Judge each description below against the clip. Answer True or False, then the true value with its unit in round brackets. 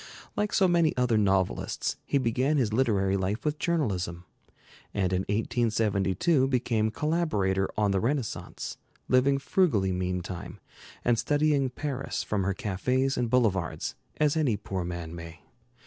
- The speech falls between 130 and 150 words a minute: True (135 wpm)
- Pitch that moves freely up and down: True (6.2 semitones)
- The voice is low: True (115 Hz)